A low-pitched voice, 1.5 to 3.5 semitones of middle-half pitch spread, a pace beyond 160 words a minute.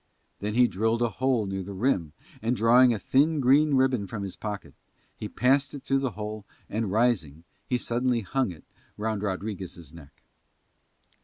No: low, 110 Hz; average, 4.5 semitones; average, 170 wpm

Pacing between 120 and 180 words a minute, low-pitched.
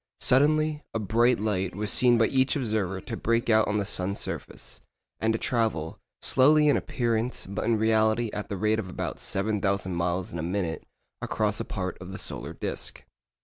No: average, 190 wpm; low, 110 Hz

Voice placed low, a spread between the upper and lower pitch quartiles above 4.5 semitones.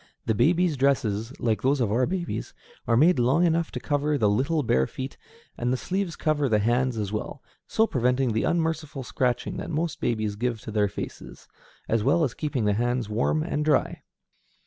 Yes: low, 130 Hz; average, 5.3 semitones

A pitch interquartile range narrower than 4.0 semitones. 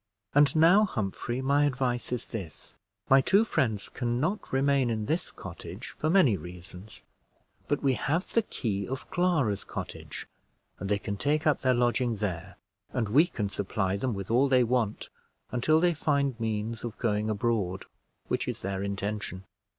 No: wide, 5.5 semitones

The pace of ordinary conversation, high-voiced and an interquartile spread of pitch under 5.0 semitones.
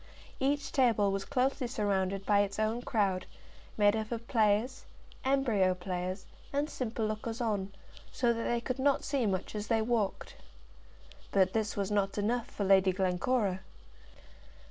Yes: average, 150 wpm; high, 215 Hz; average, 3.6 semitones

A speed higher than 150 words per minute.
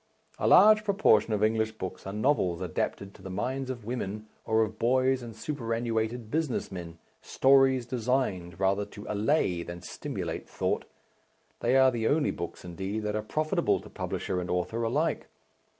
Yes: average, 165 wpm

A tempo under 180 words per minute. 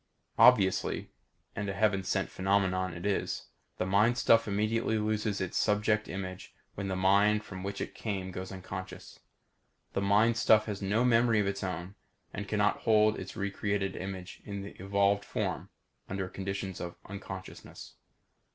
Yes: average, 155 wpm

